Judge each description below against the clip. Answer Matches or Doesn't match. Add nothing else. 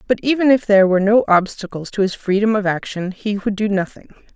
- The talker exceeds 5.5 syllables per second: Matches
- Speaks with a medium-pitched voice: Doesn't match